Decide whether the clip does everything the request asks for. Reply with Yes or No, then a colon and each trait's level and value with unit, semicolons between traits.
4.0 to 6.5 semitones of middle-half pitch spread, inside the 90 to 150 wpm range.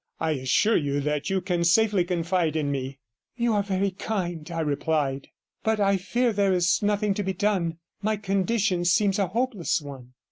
No: average, 4.3 semitones; average, 180 wpm